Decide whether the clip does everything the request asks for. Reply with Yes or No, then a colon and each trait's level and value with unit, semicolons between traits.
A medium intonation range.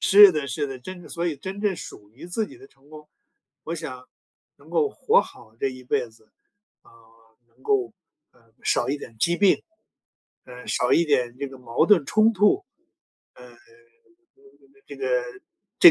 No: wide, 8.1 semitones